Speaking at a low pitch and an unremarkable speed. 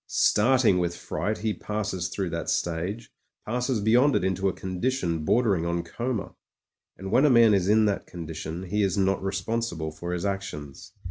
Yes: very low, 95 Hz; average, 180 wpm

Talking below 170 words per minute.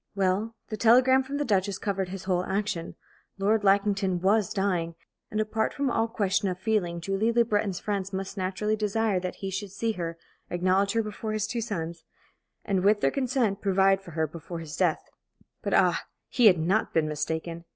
No: average, 190 wpm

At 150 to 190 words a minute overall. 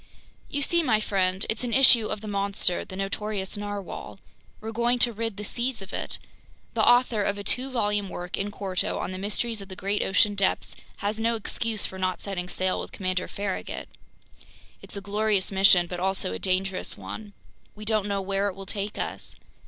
No: average, 200 wpm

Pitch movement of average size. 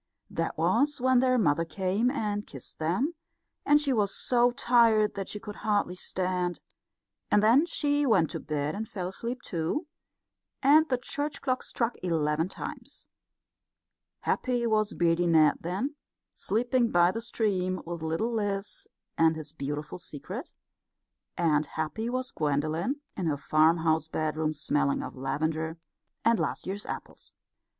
No: wide, 7.0 semitones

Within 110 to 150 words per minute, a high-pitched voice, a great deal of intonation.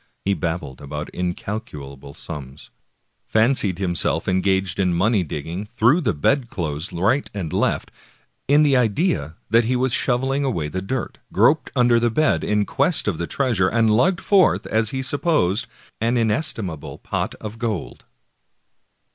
No: average, 145 wpm; low, 105 Hz; wide, 6.3 semitones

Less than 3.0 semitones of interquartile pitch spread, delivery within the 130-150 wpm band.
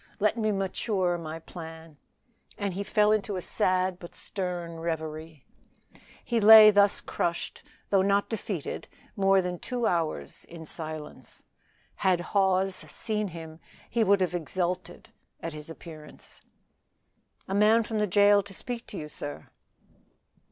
No: average, 3.8 semitones; average, 140 wpm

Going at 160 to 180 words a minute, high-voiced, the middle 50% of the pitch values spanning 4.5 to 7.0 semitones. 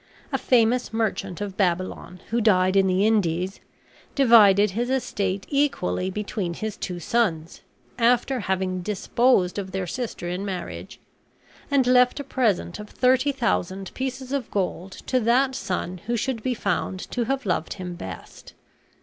No: average, 150 wpm; high, 205 Hz; average, 5.0 semitones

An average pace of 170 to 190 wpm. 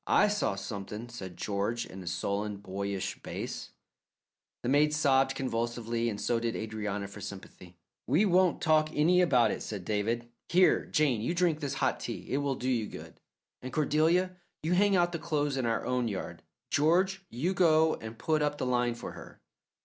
Yes: average, 185 wpm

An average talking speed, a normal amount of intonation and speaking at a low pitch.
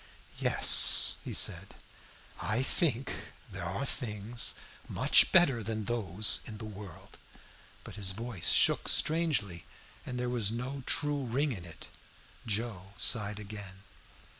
No: slow, 130 wpm; average, 3.9 semitones; low, 110 Hz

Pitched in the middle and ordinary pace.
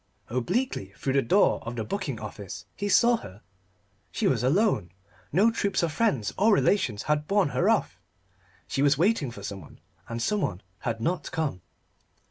Yes: medium, 145 Hz; average, 165 wpm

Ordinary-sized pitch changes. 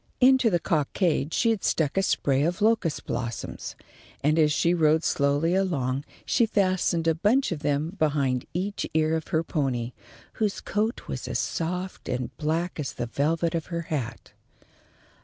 Yes: average, 4.4 semitones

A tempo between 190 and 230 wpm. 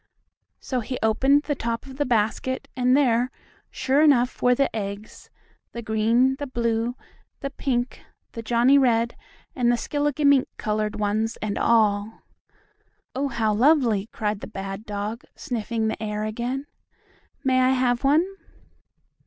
No: average, 145 wpm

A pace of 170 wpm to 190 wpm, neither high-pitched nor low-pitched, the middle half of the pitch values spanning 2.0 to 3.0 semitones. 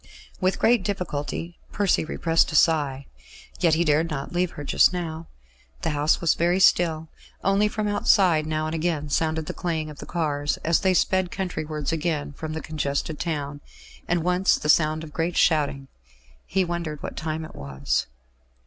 Yes: average, 175 wpm; medium, 160 Hz; average, 2.7 semitones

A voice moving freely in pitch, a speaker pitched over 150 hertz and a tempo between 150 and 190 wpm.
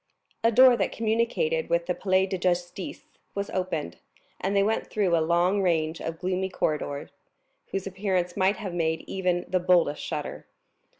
No: narrow, 2.6 semitones; medium, 185 Hz; average, 165 wpm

